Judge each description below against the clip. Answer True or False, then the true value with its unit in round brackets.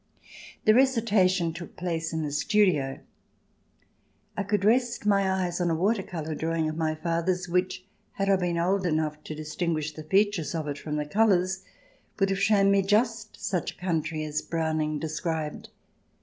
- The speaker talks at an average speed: True (175 wpm)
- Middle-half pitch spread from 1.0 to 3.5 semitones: False (3.9 semitones)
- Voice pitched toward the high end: False (175 Hz)